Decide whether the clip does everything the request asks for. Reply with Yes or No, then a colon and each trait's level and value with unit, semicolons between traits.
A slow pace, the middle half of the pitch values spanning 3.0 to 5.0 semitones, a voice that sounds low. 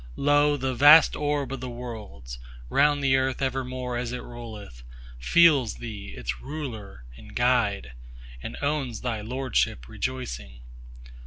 No: slow, 130 wpm; wide, 5.4 semitones; low, 125 Hz